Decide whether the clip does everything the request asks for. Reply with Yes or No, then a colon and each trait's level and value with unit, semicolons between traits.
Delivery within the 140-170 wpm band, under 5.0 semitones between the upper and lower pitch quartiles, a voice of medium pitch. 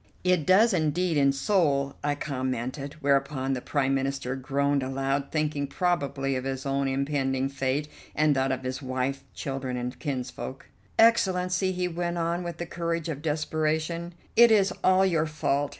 Yes: average, 160 wpm; average, 3.9 semitones; medium, 145 Hz